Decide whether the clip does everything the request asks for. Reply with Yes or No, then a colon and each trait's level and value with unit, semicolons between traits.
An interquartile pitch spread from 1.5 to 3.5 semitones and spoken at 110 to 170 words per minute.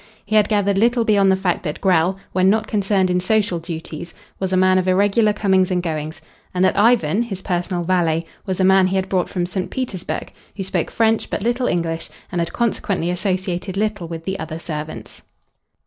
No: average, 2.7 semitones; average, 200 wpm